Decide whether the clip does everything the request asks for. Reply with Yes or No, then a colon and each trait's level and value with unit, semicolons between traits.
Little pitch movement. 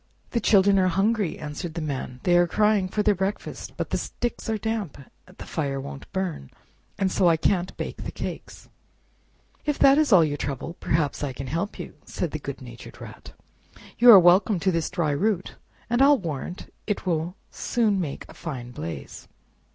No: average, 5.1 semitones